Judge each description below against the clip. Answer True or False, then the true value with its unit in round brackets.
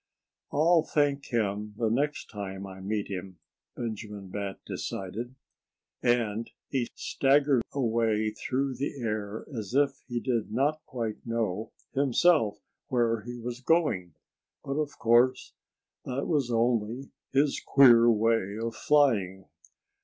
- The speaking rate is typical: False (125 wpm)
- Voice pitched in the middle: False (115 Hz)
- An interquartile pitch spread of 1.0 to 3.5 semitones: False (4.2 semitones)